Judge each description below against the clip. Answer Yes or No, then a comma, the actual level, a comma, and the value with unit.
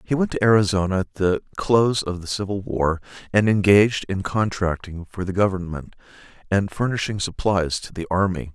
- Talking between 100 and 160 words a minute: No, average, 170 wpm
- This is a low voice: Yes, very low, 95 Hz